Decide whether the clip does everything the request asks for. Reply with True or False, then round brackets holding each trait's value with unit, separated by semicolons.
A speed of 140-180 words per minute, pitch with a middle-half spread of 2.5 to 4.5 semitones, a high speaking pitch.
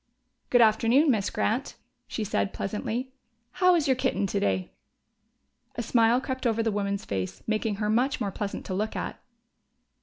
True (160 wpm; 4.0 semitones; 225 Hz)